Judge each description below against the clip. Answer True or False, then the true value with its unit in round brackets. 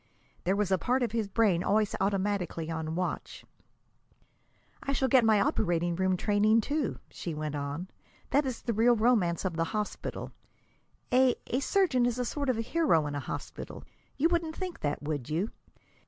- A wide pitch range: True (6.6 semitones)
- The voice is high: True (210 Hz)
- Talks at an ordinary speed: True (175 wpm)